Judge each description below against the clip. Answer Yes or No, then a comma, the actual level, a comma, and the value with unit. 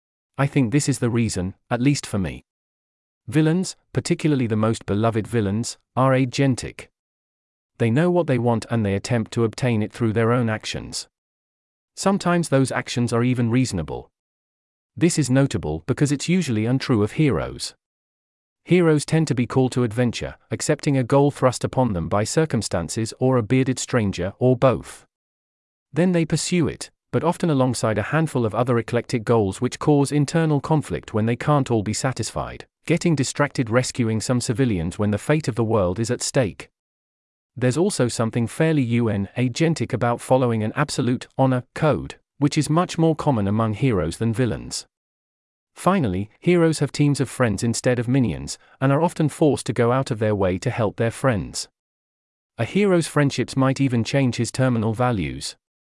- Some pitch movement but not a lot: Yes, average, 4.7 semitones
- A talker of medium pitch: No, low, 125 Hz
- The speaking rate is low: No, average, 170 wpm